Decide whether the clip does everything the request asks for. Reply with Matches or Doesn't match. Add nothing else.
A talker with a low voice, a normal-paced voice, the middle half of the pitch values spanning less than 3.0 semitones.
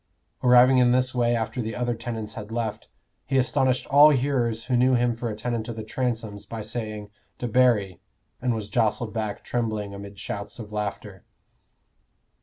Matches